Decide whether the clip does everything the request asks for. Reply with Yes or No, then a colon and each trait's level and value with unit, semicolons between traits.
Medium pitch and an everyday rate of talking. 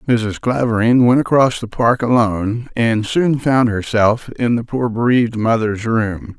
No: low, 115 Hz; average, 160 wpm